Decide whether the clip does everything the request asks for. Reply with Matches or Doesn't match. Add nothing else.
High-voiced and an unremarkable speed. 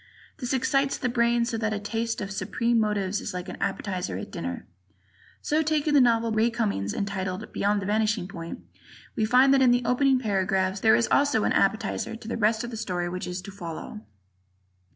Doesn't match